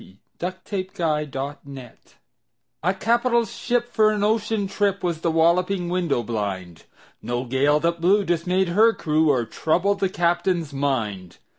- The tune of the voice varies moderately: No, wide, 6.0 semitones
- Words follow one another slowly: No, average, 150 wpm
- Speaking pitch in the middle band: Yes, medium, 170 Hz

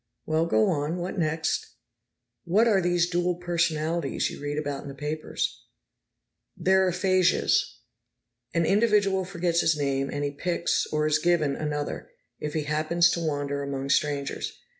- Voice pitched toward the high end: No, medium, 160 Hz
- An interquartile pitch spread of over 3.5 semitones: No, average, 3.2 semitones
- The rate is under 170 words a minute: Yes, average, 150 wpm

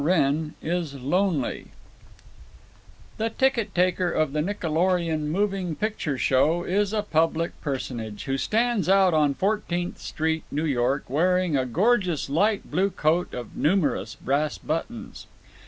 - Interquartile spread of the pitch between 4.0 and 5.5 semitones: Yes, average, 4.8 semitones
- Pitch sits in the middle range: Yes, medium, 165 Hz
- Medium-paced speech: No, slow, 130 wpm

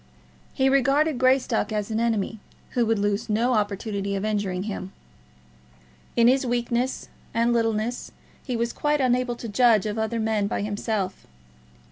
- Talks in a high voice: Yes, high, 225 Hz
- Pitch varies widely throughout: No, average, 2.9 semitones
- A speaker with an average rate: Yes, average, 150 wpm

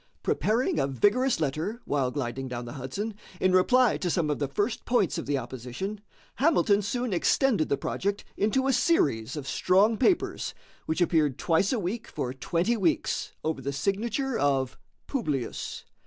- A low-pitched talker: No, medium, 180 Hz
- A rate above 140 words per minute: Yes, average, 165 wpm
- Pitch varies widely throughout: Yes, wide, 8.4 semitones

